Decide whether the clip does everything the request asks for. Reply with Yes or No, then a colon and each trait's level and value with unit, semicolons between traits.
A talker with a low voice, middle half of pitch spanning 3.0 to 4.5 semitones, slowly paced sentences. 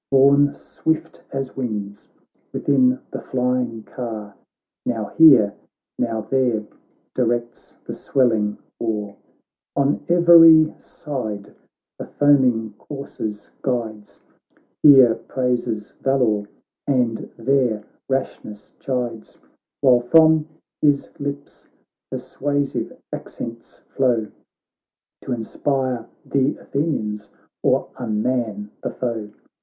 Yes: low, 125 Hz; average, 4.0 semitones; slow, 95 wpm